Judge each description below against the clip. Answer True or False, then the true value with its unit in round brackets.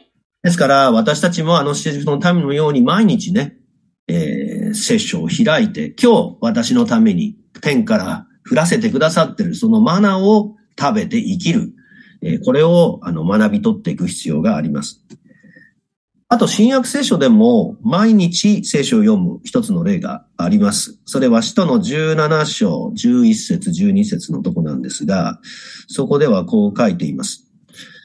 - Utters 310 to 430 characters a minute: False (295 characters per minute)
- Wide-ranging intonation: False (3.4 semitones)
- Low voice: False (215 Hz)